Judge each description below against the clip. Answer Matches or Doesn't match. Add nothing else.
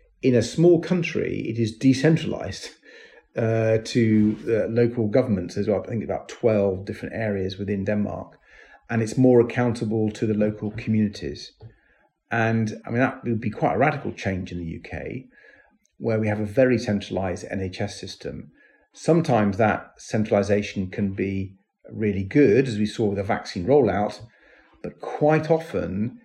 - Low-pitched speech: Matches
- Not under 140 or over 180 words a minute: Matches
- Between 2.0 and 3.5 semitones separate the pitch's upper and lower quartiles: Matches